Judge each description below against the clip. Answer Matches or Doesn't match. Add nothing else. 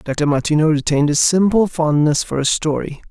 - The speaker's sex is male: Matches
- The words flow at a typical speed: Matches